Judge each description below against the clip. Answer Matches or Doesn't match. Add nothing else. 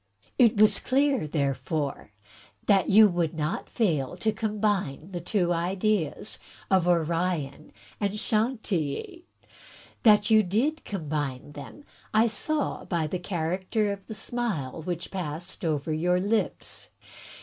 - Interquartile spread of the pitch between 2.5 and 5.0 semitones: Doesn't match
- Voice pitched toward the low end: Doesn't match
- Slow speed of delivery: Matches